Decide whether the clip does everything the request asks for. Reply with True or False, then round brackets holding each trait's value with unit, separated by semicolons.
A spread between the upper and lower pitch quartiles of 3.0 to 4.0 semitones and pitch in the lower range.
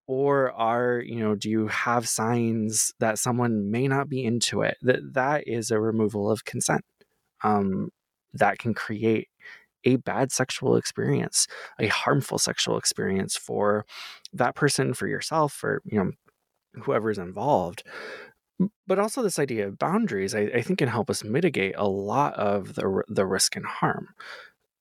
False (4.8 semitones; 115 Hz)